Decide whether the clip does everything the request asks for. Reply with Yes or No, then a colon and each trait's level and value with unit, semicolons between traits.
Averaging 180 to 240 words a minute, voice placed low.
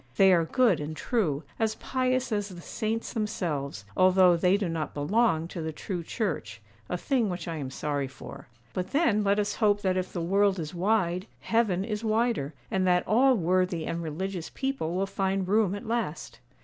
No: average, 190 wpm; medium, 185 Hz